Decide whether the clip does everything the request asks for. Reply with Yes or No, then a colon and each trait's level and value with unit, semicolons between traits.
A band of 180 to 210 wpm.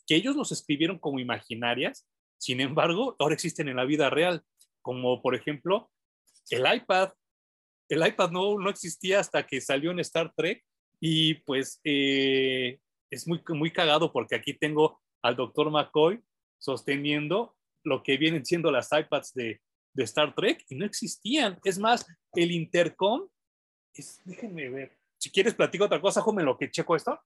No: average, 165 wpm